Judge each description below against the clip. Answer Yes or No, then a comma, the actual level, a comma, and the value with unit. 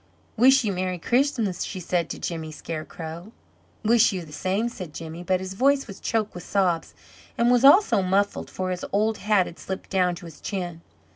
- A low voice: No, high, 190 Hz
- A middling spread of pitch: Yes, average, 4.1 semitones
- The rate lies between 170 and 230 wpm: Yes, average, 195 wpm